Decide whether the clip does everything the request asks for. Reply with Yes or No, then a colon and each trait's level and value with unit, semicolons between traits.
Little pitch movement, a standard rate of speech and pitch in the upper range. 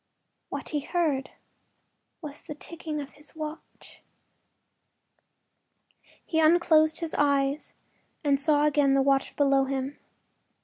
No: narrow, 2.1 semitones; slow, 115 wpm; very high, 290 Hz